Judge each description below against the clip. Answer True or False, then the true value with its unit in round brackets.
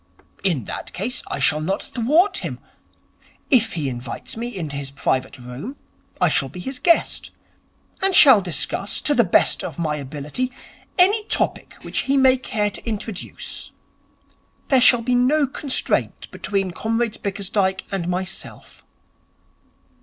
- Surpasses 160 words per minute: False (145 wpm)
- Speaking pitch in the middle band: False (205 Hz)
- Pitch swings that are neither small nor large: False (7.9 semitones)